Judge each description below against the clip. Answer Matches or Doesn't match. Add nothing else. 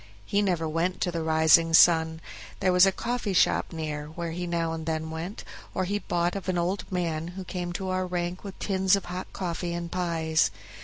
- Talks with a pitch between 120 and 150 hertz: Doesn't match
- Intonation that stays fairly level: Matches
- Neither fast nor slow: Doesn't match